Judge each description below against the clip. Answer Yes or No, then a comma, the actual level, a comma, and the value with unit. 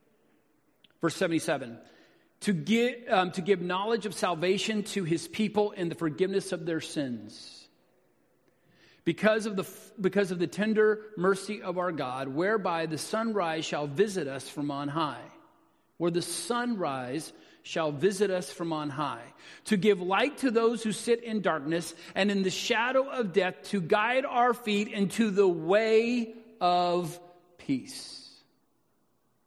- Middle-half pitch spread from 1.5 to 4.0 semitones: No, average, 4.4 semitones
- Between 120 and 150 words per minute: Yes, average, 145 wpm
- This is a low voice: No, high, 195 Hz